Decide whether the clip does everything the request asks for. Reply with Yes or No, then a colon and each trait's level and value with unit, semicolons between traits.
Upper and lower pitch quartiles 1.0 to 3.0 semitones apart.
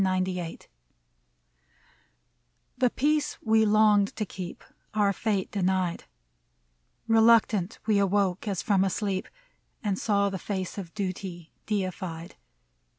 Yes: narrow, 2.4 semitones